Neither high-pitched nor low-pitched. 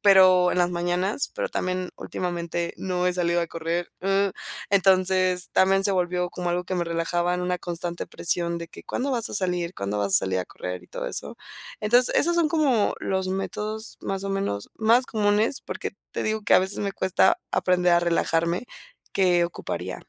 Yes: medium, 180 Hz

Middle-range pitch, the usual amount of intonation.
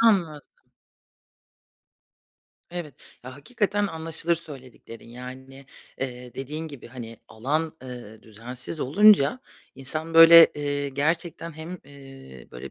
Yes: medium, 145 Hz; average, 4.4 semitones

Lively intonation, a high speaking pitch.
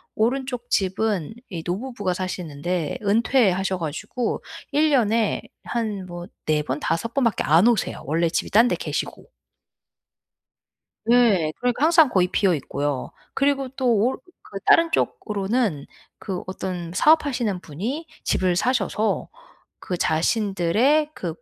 Yes: wide, 5.9 semitones; high, 205 Hz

